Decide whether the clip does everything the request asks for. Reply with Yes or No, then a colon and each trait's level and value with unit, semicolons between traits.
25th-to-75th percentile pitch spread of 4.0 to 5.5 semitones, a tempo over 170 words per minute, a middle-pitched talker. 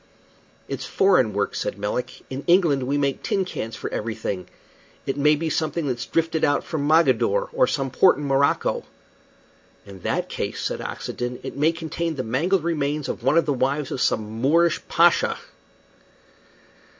No: average, 4.6 semitones; average, 165 wpm; medium, 145 Hz